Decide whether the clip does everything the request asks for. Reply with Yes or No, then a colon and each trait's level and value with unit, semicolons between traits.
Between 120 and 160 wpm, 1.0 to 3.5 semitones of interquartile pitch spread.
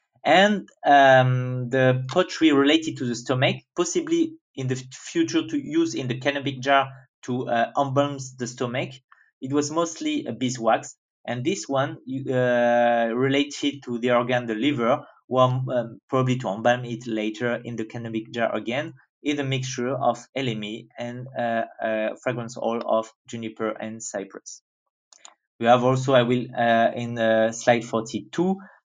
Yes: average, 155 wpm; average, 3.0 semitones